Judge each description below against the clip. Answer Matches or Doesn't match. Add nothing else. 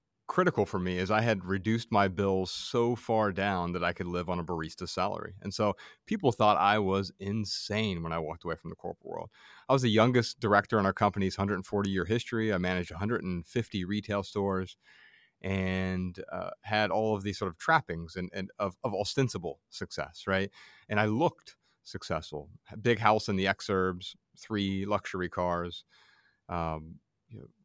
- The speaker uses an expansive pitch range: Doesn't match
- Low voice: Matches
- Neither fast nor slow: Matches